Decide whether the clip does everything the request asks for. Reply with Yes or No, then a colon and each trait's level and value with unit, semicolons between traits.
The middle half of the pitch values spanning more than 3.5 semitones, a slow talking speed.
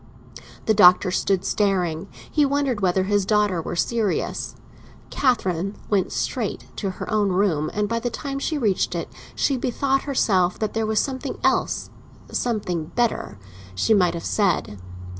No: average, 4.4 semitones; average, 145 wpm